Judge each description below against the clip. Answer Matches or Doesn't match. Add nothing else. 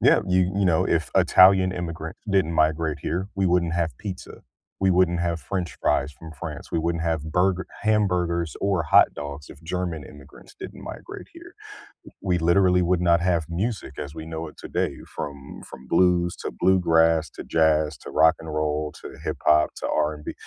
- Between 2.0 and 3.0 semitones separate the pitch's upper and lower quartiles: Matches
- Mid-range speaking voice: Doesn't match